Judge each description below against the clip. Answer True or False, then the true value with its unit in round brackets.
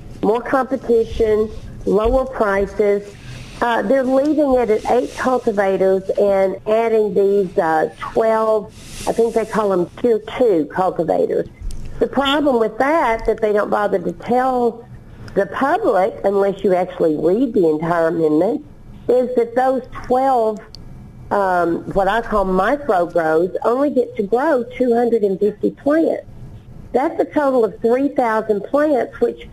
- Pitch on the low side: False (225 Hz)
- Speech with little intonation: False (4.0 semitones)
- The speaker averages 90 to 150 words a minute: True (135 wpm)